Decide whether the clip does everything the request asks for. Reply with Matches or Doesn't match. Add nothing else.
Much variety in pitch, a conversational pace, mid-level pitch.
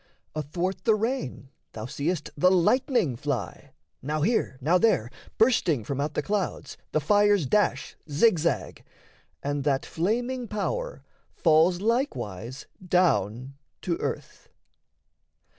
Doesn't match